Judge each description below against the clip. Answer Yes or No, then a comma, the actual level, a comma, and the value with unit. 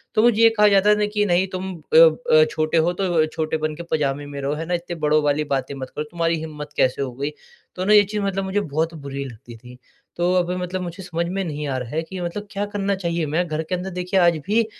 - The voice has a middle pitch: Yes, medium, 170 Hz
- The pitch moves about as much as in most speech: Yes, average, 4.2 semitones